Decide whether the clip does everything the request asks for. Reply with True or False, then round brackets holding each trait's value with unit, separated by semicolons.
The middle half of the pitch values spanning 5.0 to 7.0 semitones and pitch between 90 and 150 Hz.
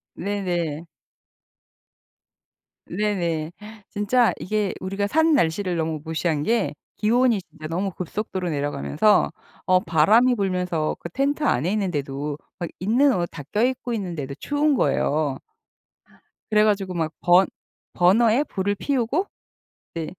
False (5.3 semitones; 185 Hz)